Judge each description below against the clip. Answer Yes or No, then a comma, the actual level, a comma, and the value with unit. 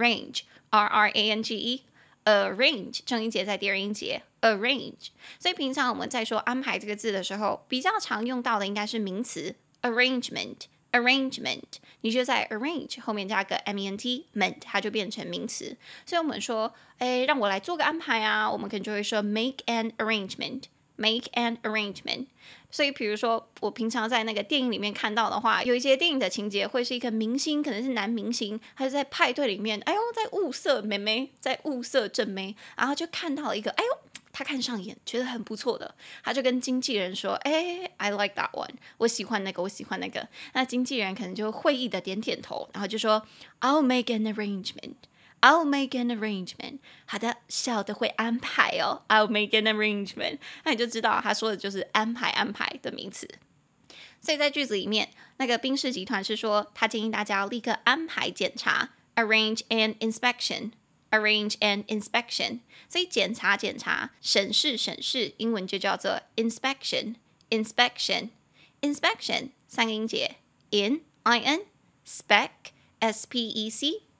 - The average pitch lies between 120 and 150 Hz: No, high, 230 Hz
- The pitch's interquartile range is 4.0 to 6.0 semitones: No, average, 3.4 semitones